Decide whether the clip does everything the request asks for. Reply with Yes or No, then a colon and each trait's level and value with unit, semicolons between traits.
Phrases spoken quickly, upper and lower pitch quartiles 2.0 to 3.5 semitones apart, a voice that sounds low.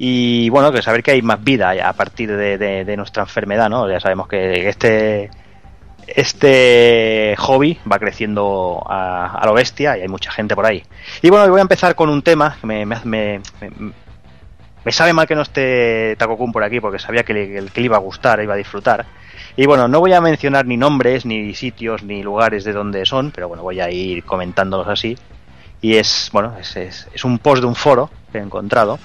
No: fast, 215 wpm; average, 4.0 semitones; low, 110 Hz